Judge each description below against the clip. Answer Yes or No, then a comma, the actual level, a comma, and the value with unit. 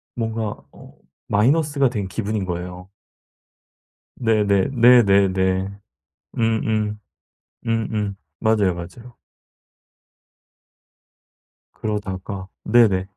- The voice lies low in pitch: Yes, low, 105 Hz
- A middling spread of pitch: Yes, average, 3.0 semitones